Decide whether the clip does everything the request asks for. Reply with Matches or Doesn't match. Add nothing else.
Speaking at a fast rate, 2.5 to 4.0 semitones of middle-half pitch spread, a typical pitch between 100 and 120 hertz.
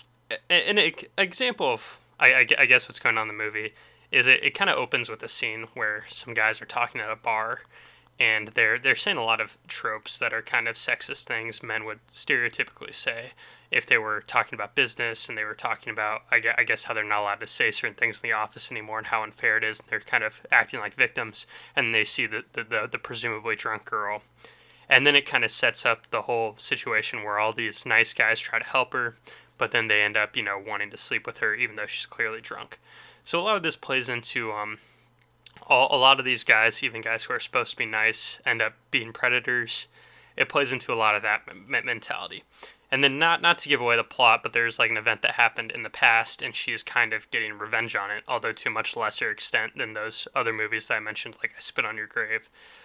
Matches